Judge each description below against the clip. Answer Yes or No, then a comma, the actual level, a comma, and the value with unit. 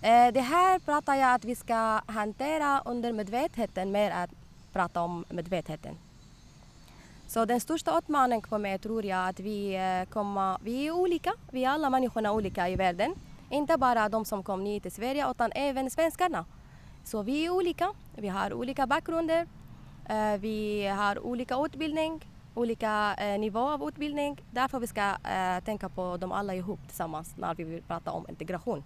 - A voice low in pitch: No, high, 225 Hz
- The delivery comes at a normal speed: Yes, average, 160 wpm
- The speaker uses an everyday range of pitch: No, wide, 6.0 semitones